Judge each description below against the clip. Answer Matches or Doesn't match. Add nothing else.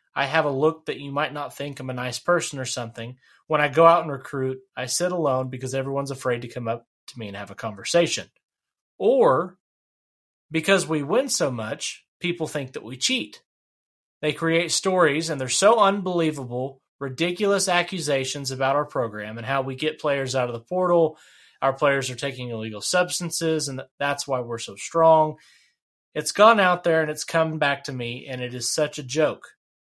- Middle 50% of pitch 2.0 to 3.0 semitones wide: Doesn't match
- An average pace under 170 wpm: Doesn't match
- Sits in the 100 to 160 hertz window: Matches